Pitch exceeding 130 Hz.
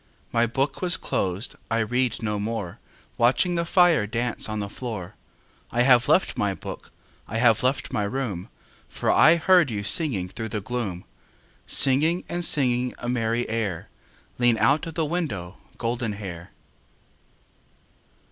No: low, 120 Hz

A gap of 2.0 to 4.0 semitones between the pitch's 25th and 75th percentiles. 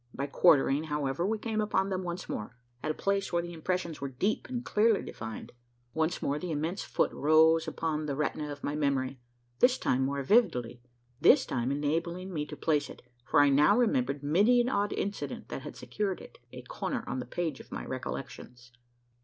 No: wide, 5.4 semitones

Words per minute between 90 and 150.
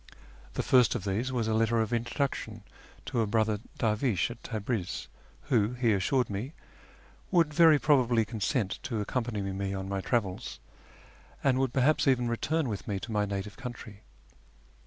No: average, 160 wpm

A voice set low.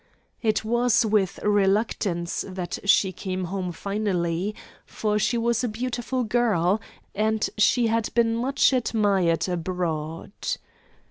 No: high, 210 Hz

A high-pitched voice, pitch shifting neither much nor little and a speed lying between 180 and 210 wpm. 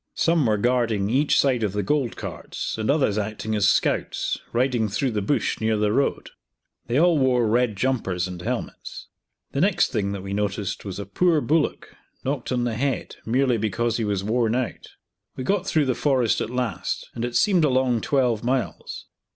No: low, 120 Hz; average, 3.9 semitones; average, 190 wpm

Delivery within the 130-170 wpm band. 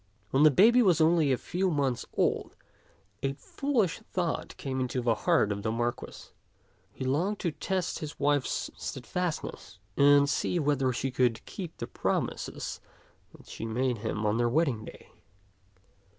Yes: average, 160 wpm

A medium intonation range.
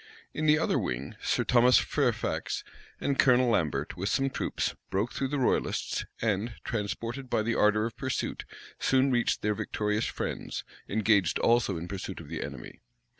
Yes: average, 4.4 semitones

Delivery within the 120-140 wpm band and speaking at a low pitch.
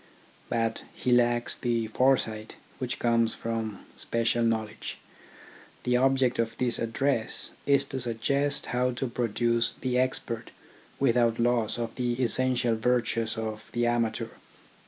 Yes: slow, 135 wpm; low, 120 Hz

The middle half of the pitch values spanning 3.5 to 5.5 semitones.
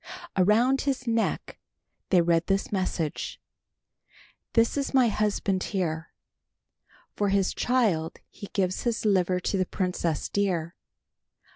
Yes: average, 3.9 semitones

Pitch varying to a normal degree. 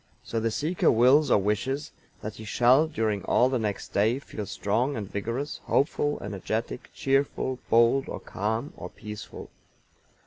Yes: average, 4.3 semitones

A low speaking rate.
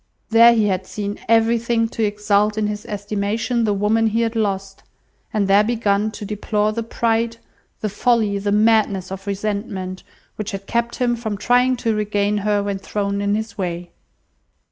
No: average, 170 wpm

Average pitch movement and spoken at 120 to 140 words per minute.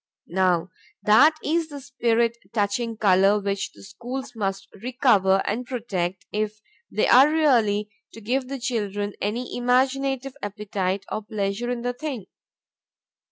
Yes: average, 4.0 semitones; slow, 135 wpm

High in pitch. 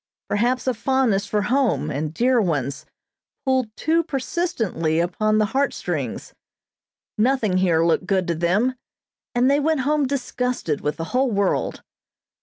Yes: high, 220 Hz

